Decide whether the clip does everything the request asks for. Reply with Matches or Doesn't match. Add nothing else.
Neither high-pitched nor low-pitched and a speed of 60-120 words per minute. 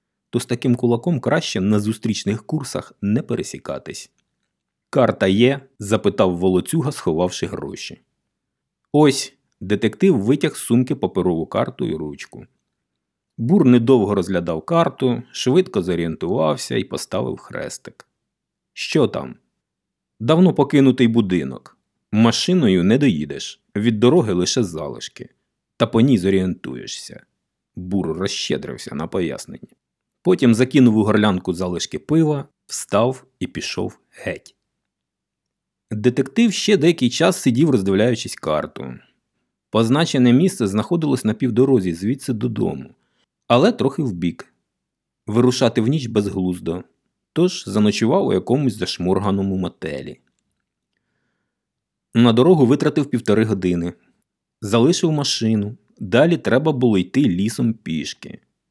Doesn't match